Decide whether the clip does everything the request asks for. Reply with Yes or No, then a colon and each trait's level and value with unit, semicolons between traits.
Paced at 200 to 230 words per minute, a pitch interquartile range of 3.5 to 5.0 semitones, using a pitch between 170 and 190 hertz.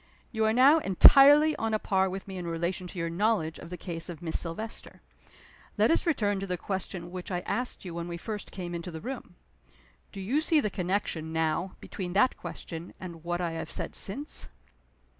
Yes: fast, 205 wpm; average, 4.2 semitones; medium, 185 Hz